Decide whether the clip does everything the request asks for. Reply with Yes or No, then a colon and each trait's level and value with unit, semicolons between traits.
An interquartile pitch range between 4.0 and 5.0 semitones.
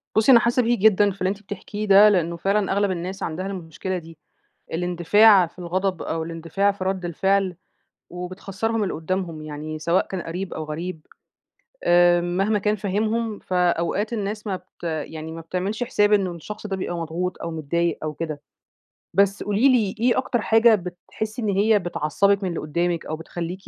No: average, 3.3 semitones